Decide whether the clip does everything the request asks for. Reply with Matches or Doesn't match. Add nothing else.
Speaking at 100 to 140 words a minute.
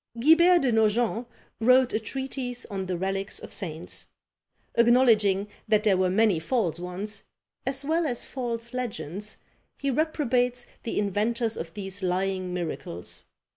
Matches